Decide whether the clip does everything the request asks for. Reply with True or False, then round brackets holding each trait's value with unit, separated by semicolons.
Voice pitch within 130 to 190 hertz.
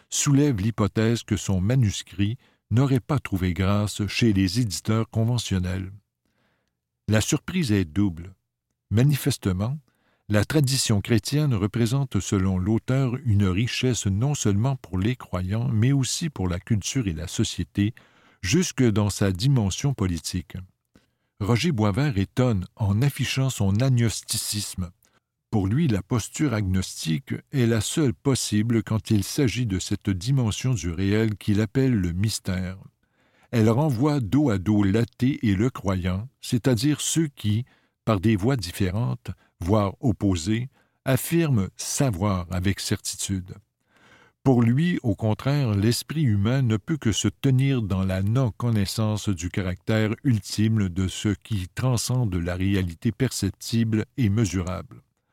False (110 Hz)